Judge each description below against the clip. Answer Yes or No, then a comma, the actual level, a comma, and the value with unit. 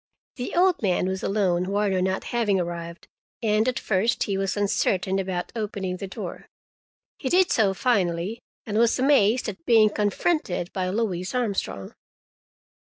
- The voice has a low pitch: No, high, 200 Hz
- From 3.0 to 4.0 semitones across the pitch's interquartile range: Yes, average, 3.5 semitones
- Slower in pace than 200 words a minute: Yes, average, 150 wpm